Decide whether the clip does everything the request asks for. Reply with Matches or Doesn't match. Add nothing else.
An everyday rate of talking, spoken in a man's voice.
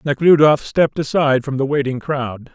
Matches